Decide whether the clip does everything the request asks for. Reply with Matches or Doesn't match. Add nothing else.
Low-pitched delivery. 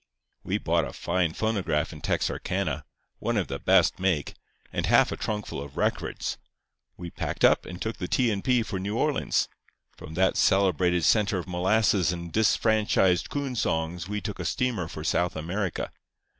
Matches